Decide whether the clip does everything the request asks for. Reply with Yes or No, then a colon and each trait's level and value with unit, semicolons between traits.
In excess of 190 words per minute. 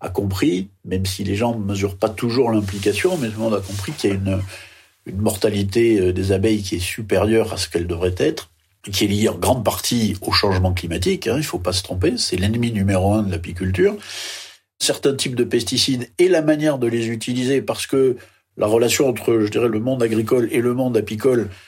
Yes: fast, 220 wpm